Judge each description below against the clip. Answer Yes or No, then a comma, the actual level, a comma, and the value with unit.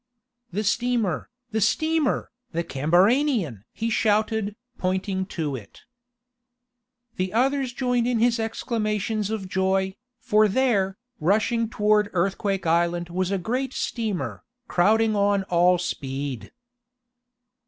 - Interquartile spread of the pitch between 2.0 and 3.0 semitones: No, average, 4.0 semitones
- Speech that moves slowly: Yes, slow, 110 wpm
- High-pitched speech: Yes, high, 205 Hz